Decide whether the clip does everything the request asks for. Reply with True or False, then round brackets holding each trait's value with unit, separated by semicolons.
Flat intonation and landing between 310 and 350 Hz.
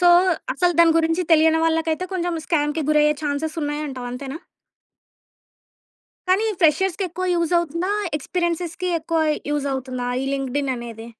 False (3.2 semitones; 320 Hz)